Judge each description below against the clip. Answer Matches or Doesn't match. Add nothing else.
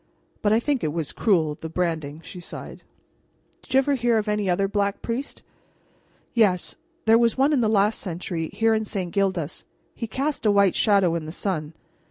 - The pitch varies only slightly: Doesn't match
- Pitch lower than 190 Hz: Doesn't match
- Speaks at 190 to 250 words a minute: Matches